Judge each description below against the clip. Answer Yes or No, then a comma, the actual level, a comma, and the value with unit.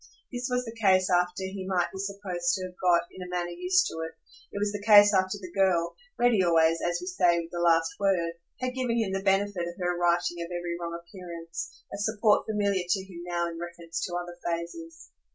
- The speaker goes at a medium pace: No, fast, 225 wpm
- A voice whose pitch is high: No, medium, 180 Hz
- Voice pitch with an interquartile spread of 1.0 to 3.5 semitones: Yes, average, 2.8 semitones